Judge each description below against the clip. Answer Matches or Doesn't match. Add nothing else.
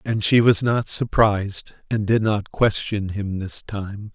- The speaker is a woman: Doesn't match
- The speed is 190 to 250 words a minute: Doesn't match